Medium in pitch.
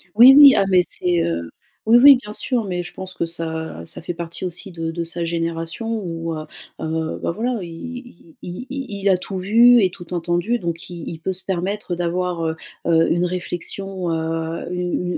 Yes: medium, 175 Hz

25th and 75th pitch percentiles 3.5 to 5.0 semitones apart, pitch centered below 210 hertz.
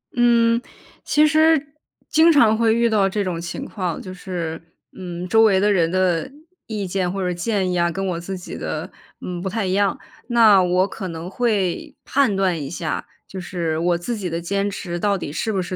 Yes: average, 4.0 semitones; high, 190 Hz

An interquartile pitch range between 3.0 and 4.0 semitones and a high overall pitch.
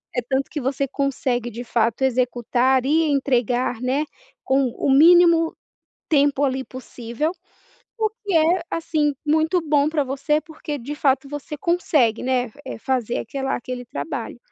Yes: average, 3.4 semitones; very high, 275 Hz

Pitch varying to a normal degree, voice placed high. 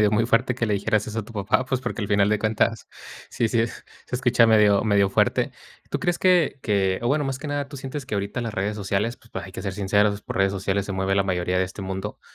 No: average, 3.4 semitones; low, 105 Hz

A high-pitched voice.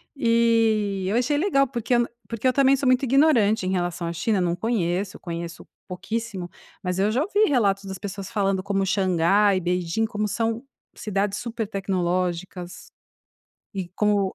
Yes: high, 205 Hz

